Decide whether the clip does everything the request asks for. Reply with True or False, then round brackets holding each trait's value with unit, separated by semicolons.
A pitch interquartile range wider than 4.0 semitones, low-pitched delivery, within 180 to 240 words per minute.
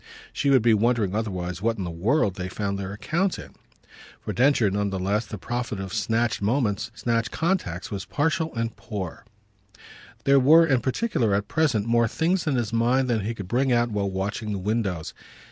True (4.4 semitones; 115 Hz; 195 wpm)